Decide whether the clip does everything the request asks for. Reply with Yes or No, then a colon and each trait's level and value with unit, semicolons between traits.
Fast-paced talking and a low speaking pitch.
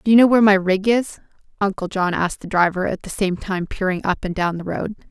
No: fast, 260 wpm; high, 195 Hz